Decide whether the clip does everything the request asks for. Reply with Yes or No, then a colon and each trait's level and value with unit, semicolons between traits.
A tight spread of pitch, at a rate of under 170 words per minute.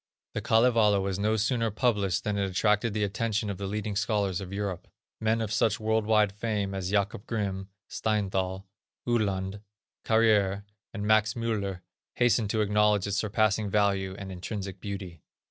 Yes: narrow, 1.9 semitones; average, 160 wpm